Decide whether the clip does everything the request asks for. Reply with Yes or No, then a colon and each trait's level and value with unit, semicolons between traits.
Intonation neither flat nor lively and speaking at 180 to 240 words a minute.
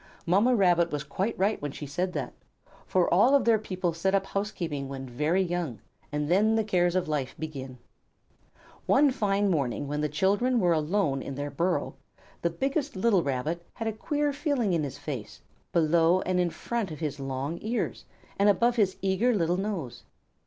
No: wide, 5.7 semitones; average, 185 wpm